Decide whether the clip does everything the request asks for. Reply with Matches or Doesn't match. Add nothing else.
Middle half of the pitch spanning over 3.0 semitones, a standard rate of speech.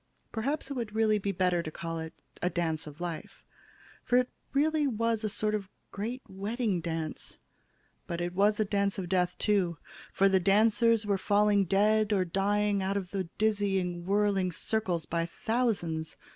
Matches